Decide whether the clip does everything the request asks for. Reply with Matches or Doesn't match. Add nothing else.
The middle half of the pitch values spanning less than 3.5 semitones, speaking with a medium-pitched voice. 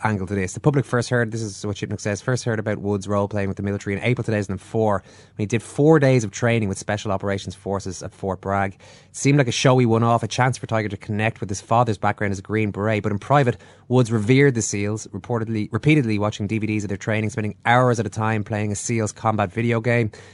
Doesn't match